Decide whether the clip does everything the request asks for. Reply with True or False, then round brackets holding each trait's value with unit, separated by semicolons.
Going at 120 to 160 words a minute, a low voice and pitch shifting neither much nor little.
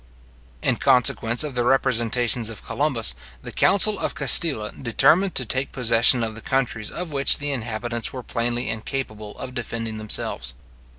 True (155 wpm; 120 Hz; 3.2 semitones)